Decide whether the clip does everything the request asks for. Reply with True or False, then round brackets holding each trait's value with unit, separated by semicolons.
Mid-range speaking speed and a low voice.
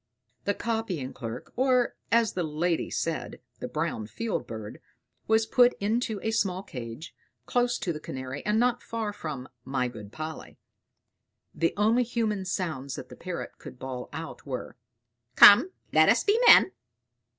False (155 wpm; 185 Hz)